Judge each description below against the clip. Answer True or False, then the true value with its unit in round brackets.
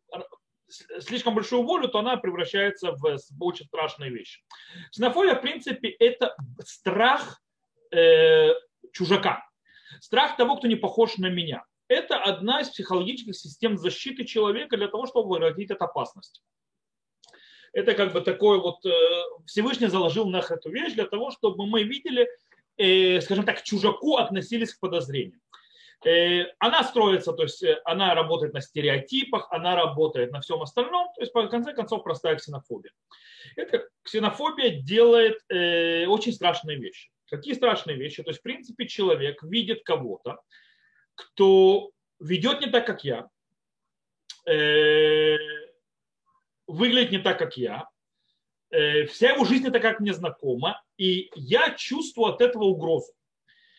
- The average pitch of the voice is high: True (230 Hz)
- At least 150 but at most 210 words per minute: False (135 wpm)